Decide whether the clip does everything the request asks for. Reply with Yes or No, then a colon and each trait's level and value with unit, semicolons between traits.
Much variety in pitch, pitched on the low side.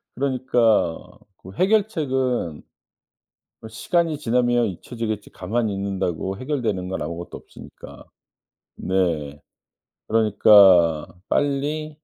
Yes: wide, 6.0 semitones; low, 115 Hz